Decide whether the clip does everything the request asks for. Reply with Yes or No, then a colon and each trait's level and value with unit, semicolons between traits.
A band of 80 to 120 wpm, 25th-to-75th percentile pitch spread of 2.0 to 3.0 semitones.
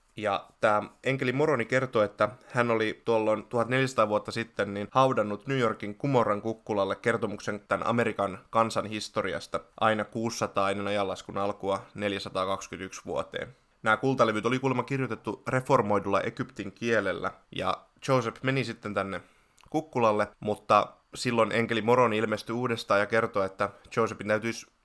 No: average, 135 wpm; average, 2.7 semitones